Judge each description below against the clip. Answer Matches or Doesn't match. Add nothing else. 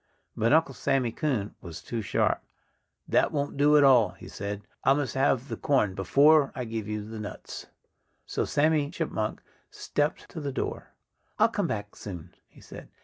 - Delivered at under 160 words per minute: Doesn't match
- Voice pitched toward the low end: Matches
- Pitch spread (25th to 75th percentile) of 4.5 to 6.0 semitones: Matches